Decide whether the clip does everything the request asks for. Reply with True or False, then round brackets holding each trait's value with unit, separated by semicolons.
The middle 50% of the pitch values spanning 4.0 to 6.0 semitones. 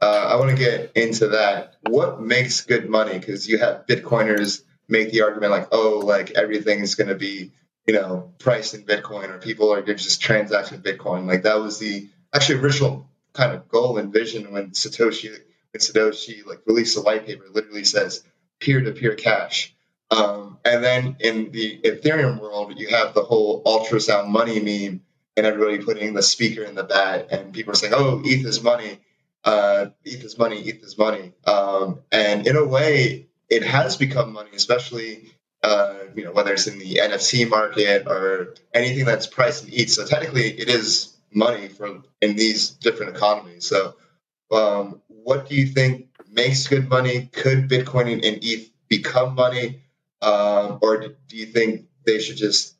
False (3.3 semitones)